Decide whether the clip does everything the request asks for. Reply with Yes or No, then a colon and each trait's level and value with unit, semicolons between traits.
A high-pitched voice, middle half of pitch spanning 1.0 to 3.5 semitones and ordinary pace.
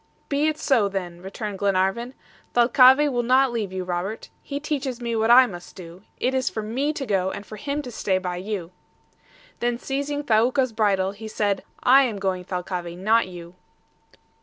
No: high, 220 Hz; average, 5.3 semitones; average, 185 wpm